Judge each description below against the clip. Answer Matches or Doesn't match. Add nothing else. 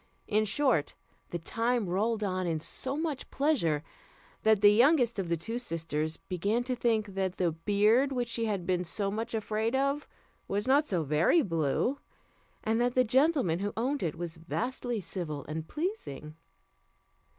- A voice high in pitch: Matches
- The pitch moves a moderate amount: Doesn't match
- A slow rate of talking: Doesn't match